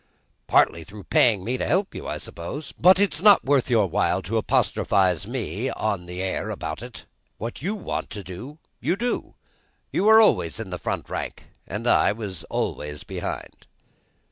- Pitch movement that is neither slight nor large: No, wide, 8.1 semitones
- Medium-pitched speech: No, low, 110 Hz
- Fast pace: No, average, 175 wpm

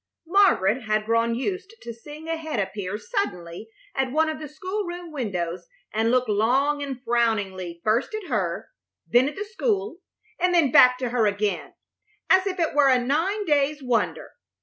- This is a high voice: Yes, very high, 260 Hz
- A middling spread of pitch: No, wide, 7.3 semitones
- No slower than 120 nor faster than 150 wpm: No, average, 175 wpm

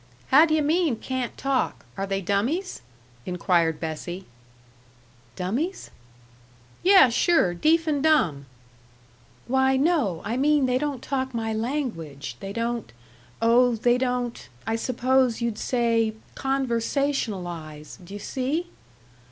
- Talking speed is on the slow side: Yes, slow, 120 wpm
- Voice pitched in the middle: No, high, 240 Hz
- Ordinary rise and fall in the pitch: No, wide, 5.7 semitones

